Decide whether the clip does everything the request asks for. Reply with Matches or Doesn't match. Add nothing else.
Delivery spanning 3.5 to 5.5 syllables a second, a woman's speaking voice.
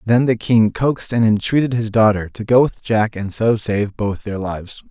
Doesn't match